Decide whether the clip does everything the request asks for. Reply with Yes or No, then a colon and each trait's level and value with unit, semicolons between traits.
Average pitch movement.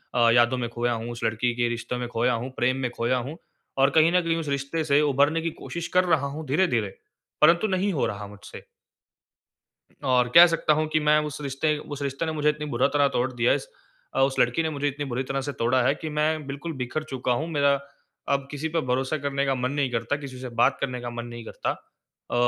Yes: average, 3.8 semitones